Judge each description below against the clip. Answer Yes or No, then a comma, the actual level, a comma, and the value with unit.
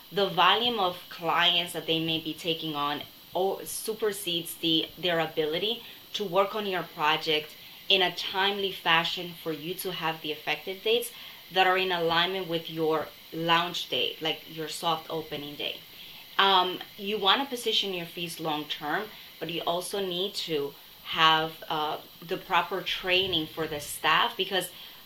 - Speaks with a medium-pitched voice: Yes, medium, 170 Hz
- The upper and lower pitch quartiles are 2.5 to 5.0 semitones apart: Yes, average, 2.9 semitones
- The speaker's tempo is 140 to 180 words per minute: Yes, average, 160 wpm